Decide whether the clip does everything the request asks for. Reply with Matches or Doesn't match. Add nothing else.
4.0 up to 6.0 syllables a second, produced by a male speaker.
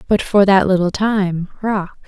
Doesn't match